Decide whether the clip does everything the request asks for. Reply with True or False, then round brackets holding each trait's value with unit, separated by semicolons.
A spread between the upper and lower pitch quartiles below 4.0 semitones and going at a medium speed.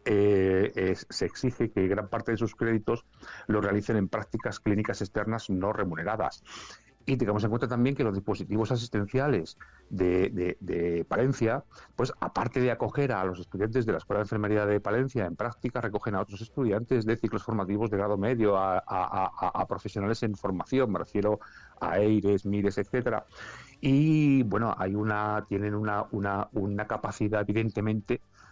True (2.4 semitones; 170 wpm)